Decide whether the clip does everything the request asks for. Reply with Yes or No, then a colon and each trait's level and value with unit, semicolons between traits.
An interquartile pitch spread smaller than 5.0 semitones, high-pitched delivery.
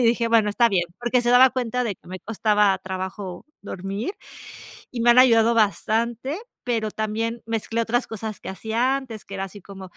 Yes: average, 2.9 semitones; high, 225 Hz